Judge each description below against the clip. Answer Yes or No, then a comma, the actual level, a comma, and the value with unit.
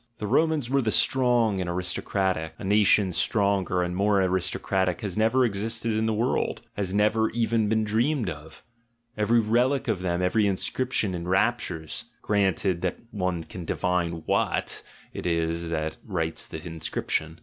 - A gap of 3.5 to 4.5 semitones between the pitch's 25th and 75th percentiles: Yes, average, 4.0 semitones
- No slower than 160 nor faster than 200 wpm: No, average, 150 wpm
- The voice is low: Yes, low, 100 Hz